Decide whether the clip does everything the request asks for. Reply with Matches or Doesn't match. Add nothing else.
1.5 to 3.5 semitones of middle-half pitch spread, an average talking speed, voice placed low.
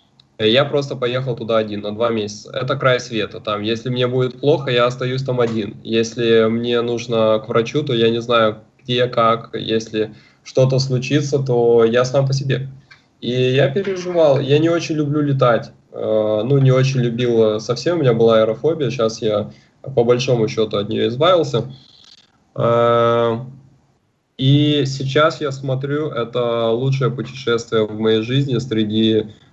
Matches